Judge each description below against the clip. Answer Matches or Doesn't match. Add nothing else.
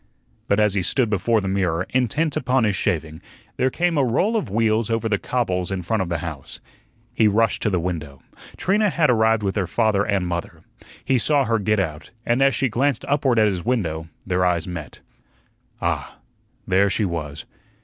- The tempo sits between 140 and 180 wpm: Doesn't match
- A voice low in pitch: Matches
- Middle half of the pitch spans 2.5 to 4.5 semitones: Doesn't match